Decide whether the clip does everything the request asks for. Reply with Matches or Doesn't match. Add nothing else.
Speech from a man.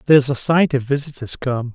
Matches